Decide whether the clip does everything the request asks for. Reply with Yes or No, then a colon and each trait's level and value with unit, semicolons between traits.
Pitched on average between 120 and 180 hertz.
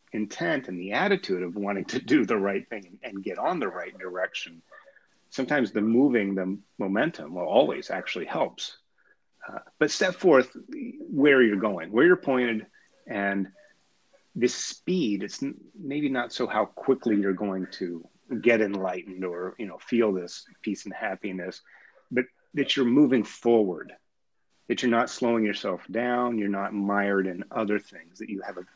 No: low, 105 Hz